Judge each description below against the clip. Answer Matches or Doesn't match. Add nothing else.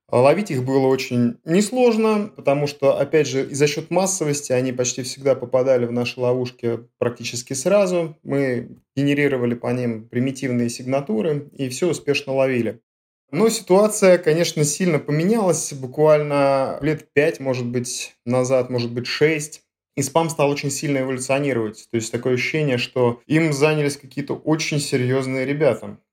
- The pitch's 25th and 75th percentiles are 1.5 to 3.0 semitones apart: Doesn't match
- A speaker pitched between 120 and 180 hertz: Matches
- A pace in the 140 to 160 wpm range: Matches